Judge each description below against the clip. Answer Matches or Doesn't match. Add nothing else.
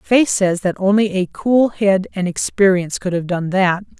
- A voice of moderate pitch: Doesn't match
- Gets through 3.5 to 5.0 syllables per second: Matches